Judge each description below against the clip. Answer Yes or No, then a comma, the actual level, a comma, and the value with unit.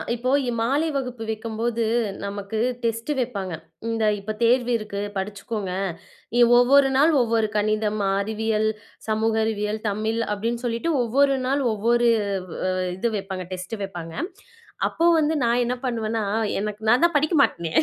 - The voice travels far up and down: No, narrow, 2.6 semitones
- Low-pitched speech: No, high, 225 Hz